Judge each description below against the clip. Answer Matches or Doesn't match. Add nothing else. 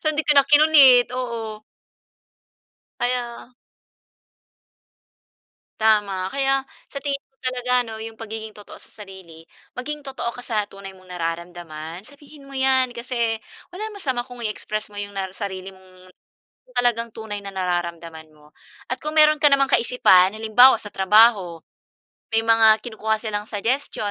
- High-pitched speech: Matches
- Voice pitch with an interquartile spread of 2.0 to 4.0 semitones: Doesn't match